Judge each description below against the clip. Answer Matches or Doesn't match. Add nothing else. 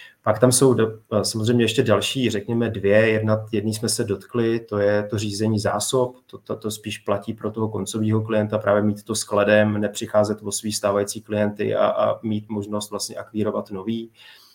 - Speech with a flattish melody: Matches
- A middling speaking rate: Doesn't match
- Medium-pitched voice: Doesn't match